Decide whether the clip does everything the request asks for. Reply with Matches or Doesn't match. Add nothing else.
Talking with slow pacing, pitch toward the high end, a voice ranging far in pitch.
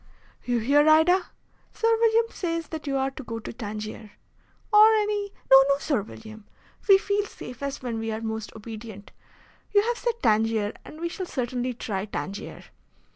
Doesn't match